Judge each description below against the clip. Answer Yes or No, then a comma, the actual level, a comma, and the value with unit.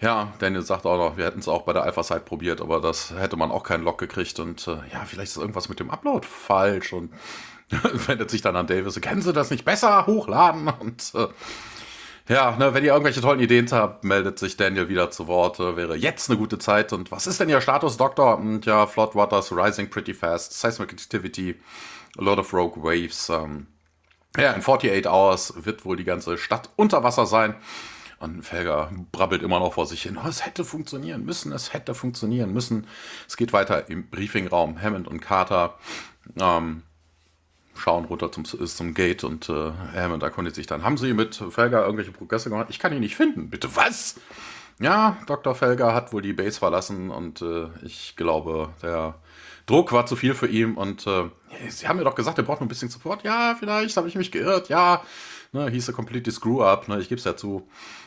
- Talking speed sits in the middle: No, fast, 210 wpm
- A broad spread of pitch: Yes, wide, 6.1 semitones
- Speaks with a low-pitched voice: Yes, low, 105 Hz